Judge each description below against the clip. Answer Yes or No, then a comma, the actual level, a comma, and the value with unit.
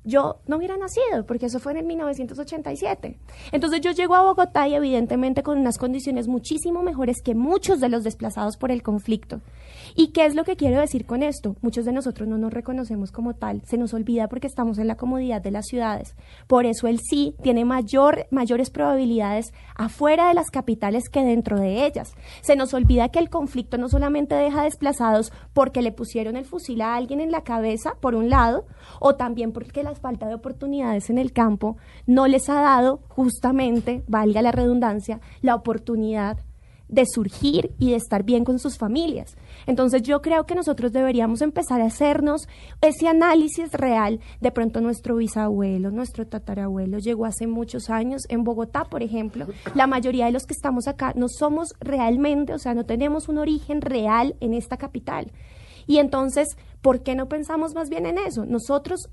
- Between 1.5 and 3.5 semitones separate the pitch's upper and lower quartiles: No, average, 3.9 semitones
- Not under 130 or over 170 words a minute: No, average, 185 wpm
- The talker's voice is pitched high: Yes, very high, 255 Hz